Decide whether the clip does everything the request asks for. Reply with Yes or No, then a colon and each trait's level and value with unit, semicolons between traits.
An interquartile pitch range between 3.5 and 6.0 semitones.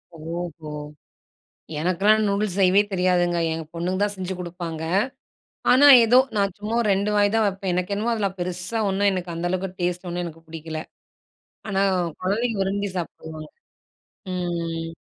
No: average, 2.7 semitones